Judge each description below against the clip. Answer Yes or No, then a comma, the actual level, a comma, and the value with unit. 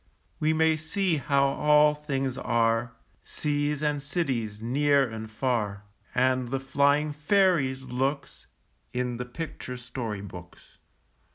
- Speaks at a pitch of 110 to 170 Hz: Yes, low, 135 Hz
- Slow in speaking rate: Yes, slow, 120 wpm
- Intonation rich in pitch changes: No, average, 3.5 semitones